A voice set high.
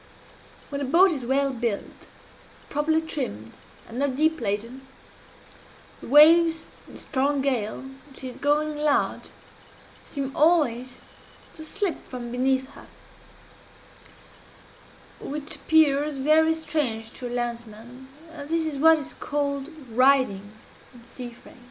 Yes: very high, 275 Hz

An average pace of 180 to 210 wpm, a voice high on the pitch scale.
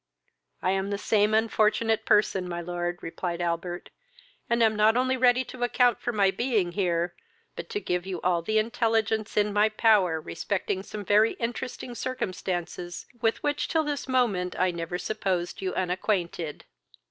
No: average, 160 wpm; high, 205 Hz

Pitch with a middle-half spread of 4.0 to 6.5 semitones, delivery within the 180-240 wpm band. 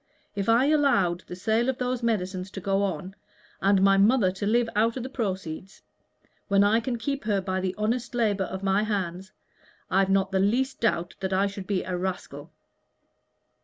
No: average, 3.4 semitones; average, 190 wpm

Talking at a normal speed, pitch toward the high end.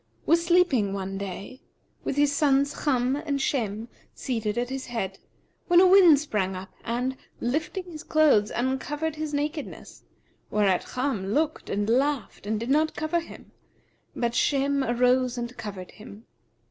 Yes: average, 150 wpm; very high, 260 Hz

